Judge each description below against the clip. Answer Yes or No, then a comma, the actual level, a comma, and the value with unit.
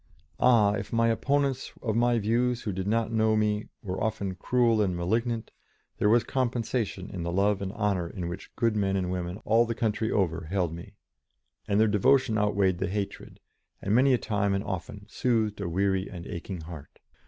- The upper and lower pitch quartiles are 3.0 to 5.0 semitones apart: Yes, average, 3.4 semitones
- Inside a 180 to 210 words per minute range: Yes, average, 190 wpm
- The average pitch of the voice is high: No, low, 105 Hz